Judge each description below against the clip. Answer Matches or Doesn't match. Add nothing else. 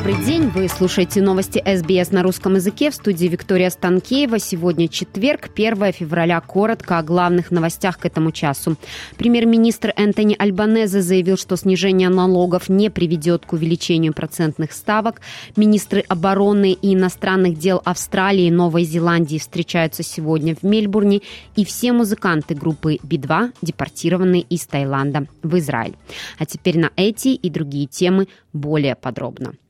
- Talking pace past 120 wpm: Matches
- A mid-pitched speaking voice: Matches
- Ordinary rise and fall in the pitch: Matches